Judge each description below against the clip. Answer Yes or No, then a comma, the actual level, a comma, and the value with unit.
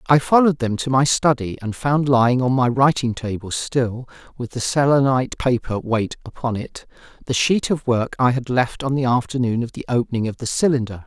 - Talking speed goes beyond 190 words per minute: Yes, average, 200 wpm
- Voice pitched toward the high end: No, low, 125 Hz